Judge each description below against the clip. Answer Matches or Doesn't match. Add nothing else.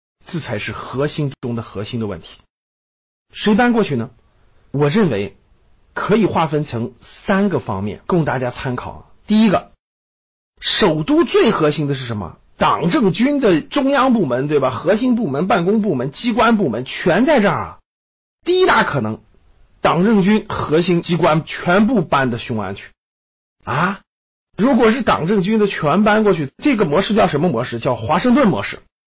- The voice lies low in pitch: Doesn't match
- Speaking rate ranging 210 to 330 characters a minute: Matches